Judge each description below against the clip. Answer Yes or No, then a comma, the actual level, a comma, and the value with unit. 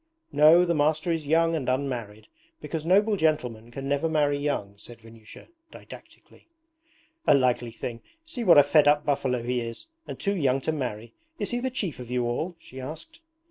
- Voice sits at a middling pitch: Yes, medium, 145 Hz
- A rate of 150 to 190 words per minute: Yes, average, 185 wpm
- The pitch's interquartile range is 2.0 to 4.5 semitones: No, average, 5.0 semitones